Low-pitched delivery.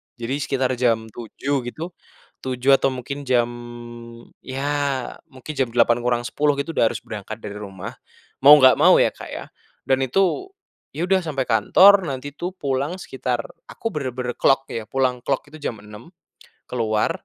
Yes: low, 130 Hz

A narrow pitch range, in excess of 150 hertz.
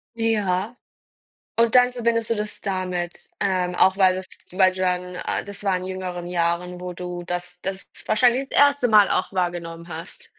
No: average, 3.0 semitones; medium, 185 Hz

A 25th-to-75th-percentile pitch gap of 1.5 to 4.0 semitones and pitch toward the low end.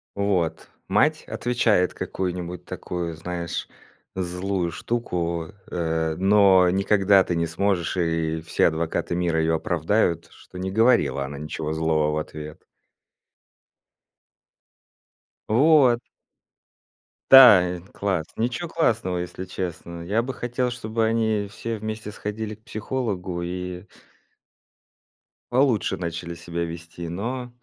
No: average, 4.4 semitones; very low, 90 Hz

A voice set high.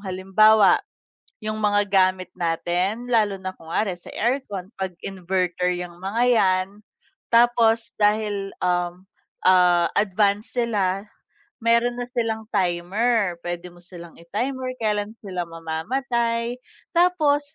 Yes: high, 200 Hz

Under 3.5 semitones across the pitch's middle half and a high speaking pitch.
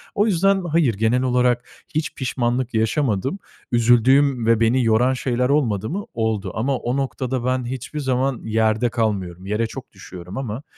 No: average, 3.1 semitones; low, 125 Hz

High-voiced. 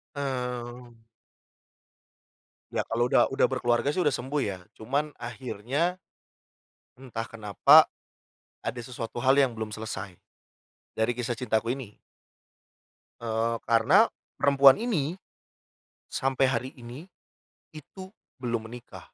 No: low, 125 Hz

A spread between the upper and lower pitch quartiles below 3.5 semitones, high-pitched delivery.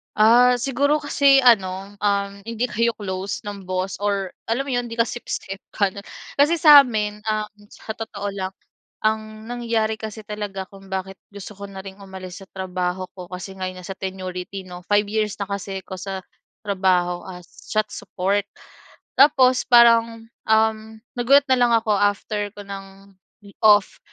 Yes: average, 3.1 semitones; high, 205 Hz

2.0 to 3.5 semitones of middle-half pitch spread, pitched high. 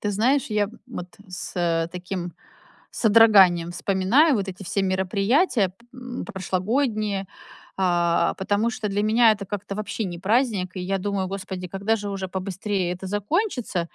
Yes: average, 2.9 semitones; high, 195 Hz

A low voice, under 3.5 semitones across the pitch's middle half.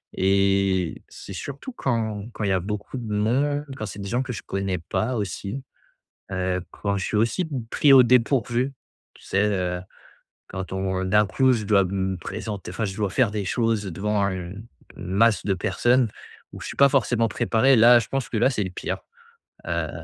No: low, 105 Hz; average, 3.9 semitones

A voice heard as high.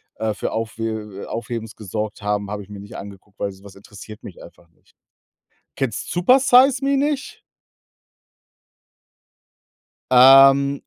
No: low, 110 Hz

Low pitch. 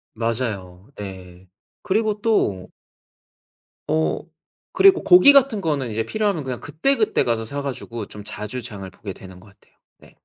Yes: low, 115 Hz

